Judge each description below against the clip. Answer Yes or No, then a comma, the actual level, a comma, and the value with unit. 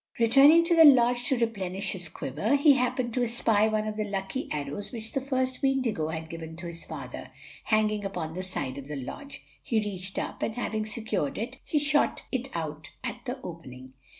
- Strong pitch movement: Yes, wide, 7.0 semitones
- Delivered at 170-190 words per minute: No, average, 200 wpm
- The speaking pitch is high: Yes, high, 215 Hz